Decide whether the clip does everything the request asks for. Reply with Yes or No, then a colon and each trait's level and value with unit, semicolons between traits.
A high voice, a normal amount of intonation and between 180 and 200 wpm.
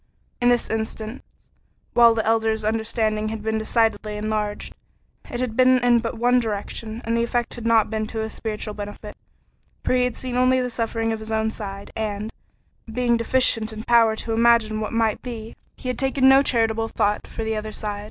No: high, 225 Hz; narrow, 1.6 semitones; average, 195 wpm